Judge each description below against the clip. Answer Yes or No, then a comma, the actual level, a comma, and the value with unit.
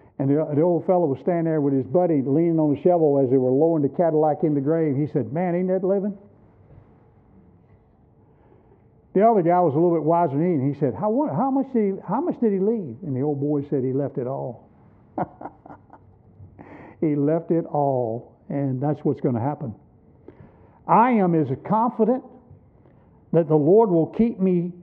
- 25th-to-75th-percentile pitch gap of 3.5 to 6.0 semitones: Yes, average, 4.5 semitones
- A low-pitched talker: No, medium, 165 Hz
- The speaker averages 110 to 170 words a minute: No, average, 200 wpm